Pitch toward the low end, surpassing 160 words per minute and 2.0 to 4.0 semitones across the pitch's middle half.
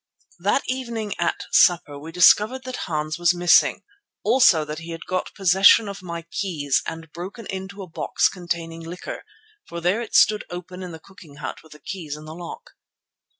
No: medium, 175 Hz; average, 185 wpm; average, 3.2 semitones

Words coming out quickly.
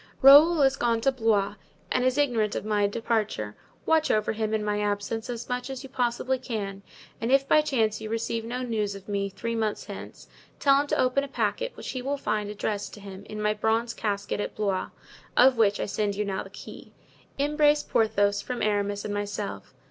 Yes: fast, 210 wpm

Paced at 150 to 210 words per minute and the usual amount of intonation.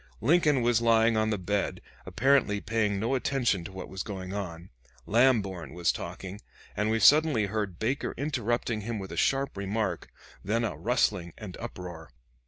Yes: average, 165 wpm; average, 3.7 semitones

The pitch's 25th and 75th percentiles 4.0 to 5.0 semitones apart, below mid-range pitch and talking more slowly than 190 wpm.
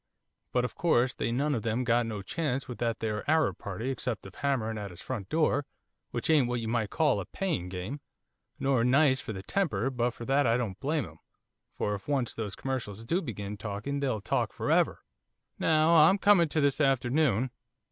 No: average, 4.7 semitones; low, 125 Hz; fast, 205 wpm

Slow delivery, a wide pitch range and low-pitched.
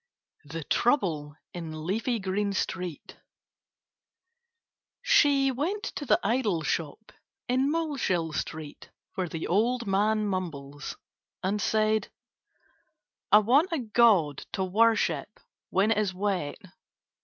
No: slow, 110 wpm; wide, 5.7 semitones; high, 205 Hz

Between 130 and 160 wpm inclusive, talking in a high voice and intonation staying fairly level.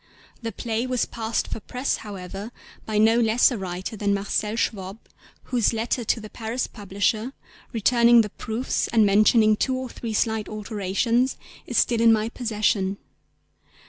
Yes: average, 155 wpm; high, 220 Hz; narrow, 2.1 semitones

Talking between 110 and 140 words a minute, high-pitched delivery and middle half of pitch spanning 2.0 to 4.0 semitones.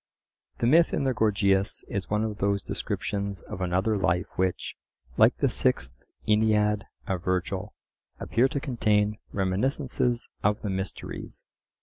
No: slow, 135 wpm; low, 105 Hz; narrow, 2.6 semitones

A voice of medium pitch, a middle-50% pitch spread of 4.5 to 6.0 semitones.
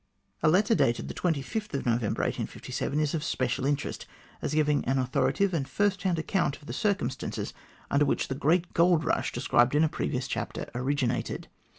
Yes: medium, 150 Hz; average, 4.8 semitones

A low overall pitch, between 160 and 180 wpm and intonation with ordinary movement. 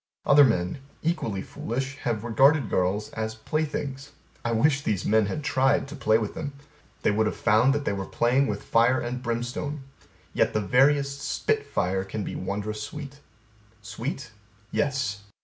Yes: low, 120 Hz; average, 165 wpm; average, 4.6 semitones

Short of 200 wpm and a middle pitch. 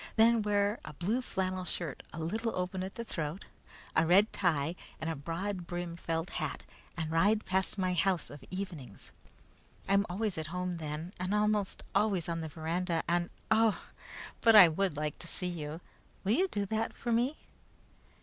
Yes: average, 180 wpm; medium, 180 Hz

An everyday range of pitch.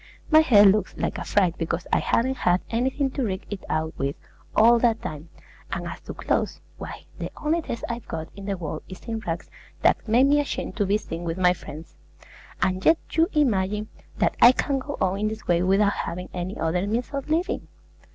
No: wide, 5.8 semitones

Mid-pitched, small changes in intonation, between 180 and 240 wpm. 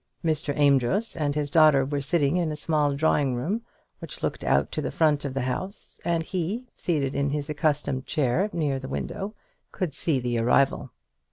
No: medium, 150 Hz; average, 3.1 semitones; average, 185 wpm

